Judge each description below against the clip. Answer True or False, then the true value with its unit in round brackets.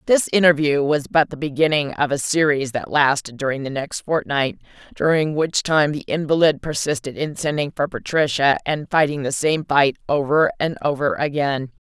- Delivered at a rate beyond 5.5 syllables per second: False (5.0 syllables/s)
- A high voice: False (145 Hz)